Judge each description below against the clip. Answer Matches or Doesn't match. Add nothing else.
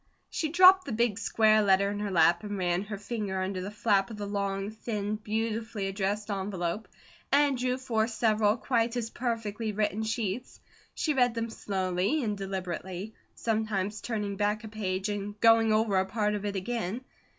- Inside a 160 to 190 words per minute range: Matches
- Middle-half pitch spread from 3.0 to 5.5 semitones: Doesn't match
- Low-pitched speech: Doesn't match